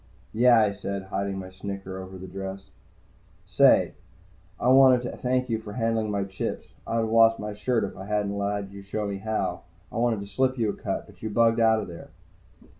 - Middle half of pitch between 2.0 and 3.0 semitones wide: Yes, narrow, 2.6 semitones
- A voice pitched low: Yes, low, 105 Hz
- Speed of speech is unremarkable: No, fast, 210 wpm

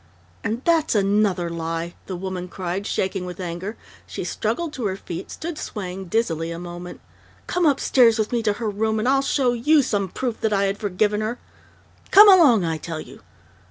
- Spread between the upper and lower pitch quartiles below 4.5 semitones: No, average, 5.0 semitones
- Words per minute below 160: No, average, 190 wpm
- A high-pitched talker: Yes, high, 205 Hz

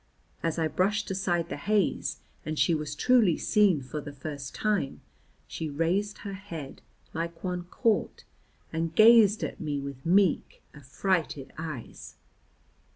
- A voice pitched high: No, medium, 165 Hz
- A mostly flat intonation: No, average, 4.8 semitones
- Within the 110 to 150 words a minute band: Yes, average, 140 wpm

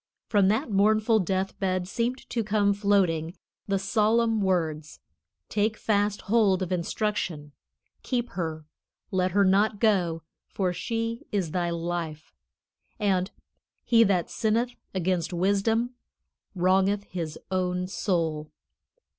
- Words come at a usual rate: No, slow, 120 wpm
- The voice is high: Yes, high, 195 Hz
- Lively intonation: No, average, 3.2 semitones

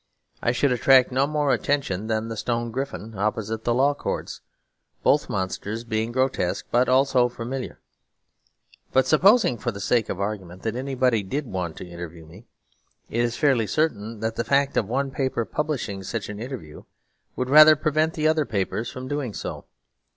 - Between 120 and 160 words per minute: No, average, 175 wpm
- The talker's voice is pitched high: No, low, 120 Hz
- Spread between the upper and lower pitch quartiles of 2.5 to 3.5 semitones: No, average, 4.2 semitones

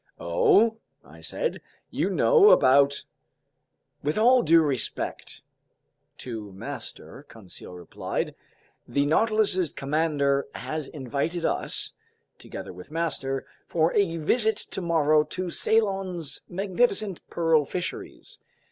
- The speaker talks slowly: Yes, slow, 105 wpm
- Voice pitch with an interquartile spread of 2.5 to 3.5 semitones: No, wide, 5.6 semitones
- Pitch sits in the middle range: Yes, medium, 165 Hz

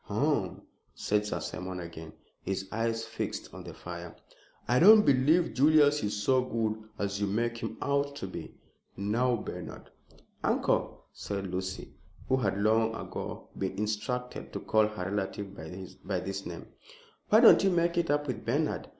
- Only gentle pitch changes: No, average, 5.2 semitones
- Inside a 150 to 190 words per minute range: Yes, average, 165 wpm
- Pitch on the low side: Yes, low, 110 Hz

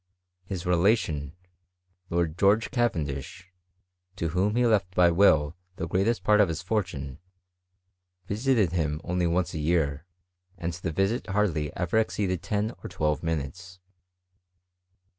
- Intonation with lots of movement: No, average, 4.1 semitones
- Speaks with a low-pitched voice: Yes, very low, 90 Hz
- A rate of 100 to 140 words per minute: Yes, slow, 135 wpm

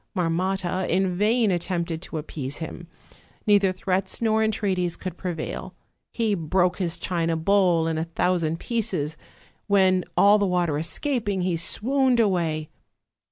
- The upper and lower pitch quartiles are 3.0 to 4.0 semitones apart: Yes, average, 3.3 semitones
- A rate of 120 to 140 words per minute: Yes, slow, 135 wpm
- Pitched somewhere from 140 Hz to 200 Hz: Yes, medium, 185 Hz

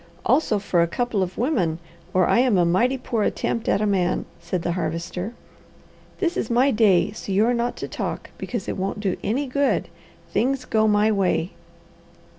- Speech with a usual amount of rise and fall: Yes, average, 4.8 semitones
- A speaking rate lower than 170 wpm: No, average, 190 wpm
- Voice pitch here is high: Yes, high, 210 Hz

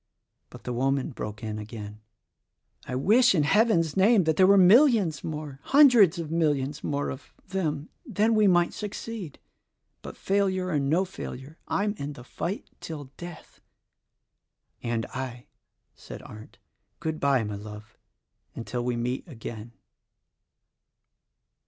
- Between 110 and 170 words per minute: Yes, slow, 135 wpm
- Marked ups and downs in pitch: Yes, wide, 7.3 semitones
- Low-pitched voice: No, medium, 150 Hz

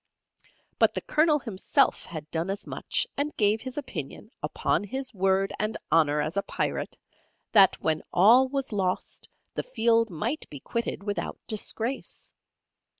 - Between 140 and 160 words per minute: Yes, average, 150 wpm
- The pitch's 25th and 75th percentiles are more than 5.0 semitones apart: Yes, wide, 5.4 semitones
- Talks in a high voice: Yes, high, 210 Hz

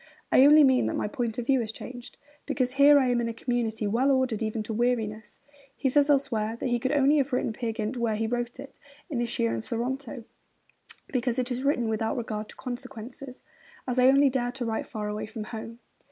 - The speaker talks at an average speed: No, fast, 220 wpm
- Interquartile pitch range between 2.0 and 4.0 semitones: Yes, average, 2.8 semitones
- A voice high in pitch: Yes, high, 245 Hz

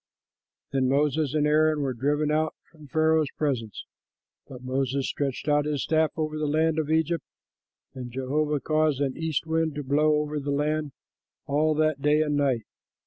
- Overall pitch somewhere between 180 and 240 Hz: No, medium, 150 Hz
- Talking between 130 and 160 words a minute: No, average, 175 wpm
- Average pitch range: No, narrow, 2.0 semitones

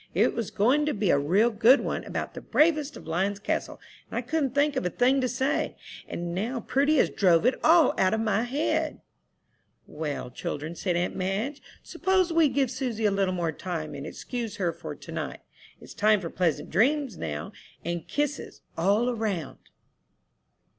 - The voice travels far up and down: Yes, wide, 7.5 semitones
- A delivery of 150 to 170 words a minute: No, average, 185 wpm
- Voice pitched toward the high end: Yes, high, 220 Hz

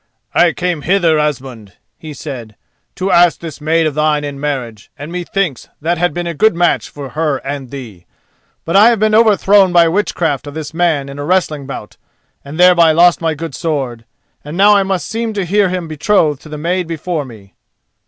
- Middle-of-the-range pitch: Yes, medium, 160 Hz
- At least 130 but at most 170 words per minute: No, average, 200 wpm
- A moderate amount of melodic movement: Yes, average, 3.8 semitones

